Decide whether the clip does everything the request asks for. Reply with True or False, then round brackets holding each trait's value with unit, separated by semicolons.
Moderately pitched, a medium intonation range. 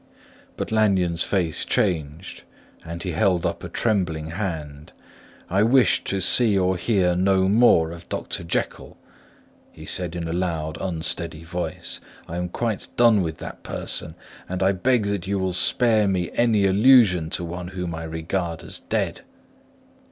False (90 Hz; 3.2 semitones)